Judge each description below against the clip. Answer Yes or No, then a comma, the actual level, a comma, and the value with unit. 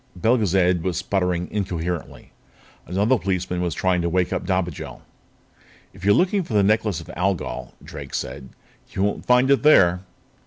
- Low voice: Yes, very low, 95 Hz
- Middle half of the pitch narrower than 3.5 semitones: Yes, average, 2.9 semitones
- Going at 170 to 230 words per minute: No, average, 155 wpm